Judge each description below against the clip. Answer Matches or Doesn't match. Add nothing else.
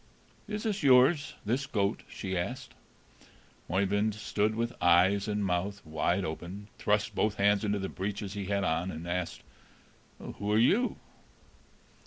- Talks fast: Doesn't match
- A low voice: Matches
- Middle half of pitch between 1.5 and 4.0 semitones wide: Matches